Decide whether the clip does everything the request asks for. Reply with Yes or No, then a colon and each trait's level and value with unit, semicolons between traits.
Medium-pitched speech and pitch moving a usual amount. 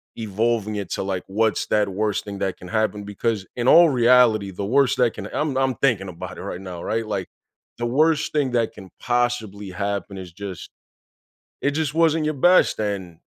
No: low, 110 Hz; average, 4.3 semitones